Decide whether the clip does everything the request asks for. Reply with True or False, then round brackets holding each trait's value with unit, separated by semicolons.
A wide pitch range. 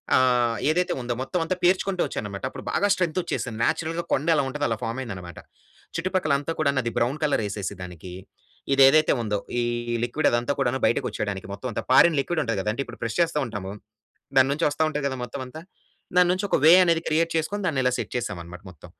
True (6.0 semitones)